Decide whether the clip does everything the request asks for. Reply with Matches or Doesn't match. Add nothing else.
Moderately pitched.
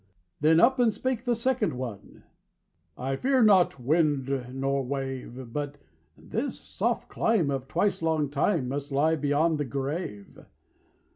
Matches